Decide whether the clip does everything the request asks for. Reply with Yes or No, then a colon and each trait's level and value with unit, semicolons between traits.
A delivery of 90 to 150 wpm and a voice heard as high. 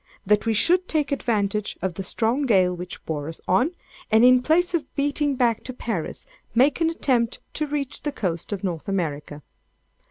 No: average, 185 wpm; high, 230 Hz